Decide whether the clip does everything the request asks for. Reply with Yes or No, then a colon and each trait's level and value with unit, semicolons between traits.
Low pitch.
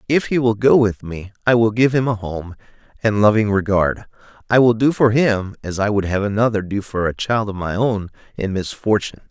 Yes: low, 105 Hz